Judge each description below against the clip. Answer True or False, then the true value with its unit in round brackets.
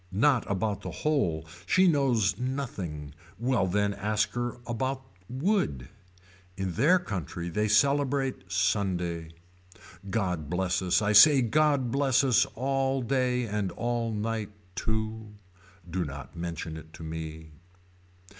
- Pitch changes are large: True (6.7 semitones)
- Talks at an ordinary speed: False (130 wpm)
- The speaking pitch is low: True (110 Hz)